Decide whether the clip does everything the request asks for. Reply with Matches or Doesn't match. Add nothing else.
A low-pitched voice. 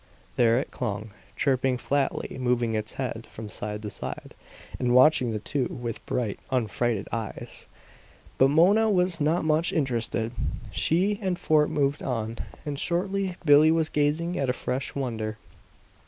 Matches